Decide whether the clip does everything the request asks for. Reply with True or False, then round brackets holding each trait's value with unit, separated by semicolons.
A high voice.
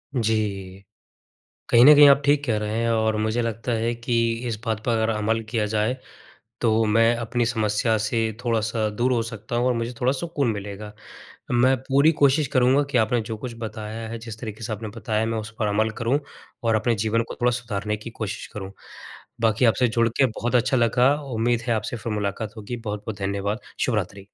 False (115 Hz)